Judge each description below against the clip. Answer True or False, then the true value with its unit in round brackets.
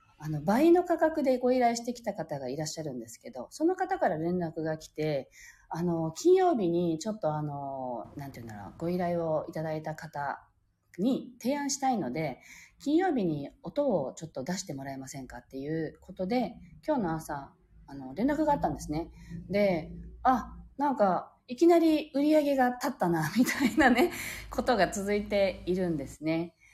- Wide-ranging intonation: True (8.8 semitones)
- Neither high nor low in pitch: True (175 Hz)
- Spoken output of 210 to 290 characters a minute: False (340 characters per minute)